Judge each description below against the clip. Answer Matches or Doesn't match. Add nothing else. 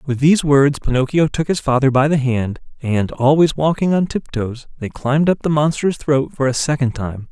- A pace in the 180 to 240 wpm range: Matches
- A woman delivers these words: Doesn't match